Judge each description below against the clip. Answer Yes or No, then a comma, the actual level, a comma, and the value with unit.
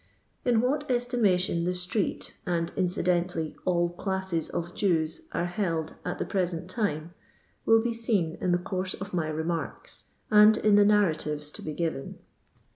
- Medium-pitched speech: Yes, medium, 180 Hz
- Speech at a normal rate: Yes, average, 155 wpm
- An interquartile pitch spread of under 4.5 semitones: Yes, average, 3.8 semitones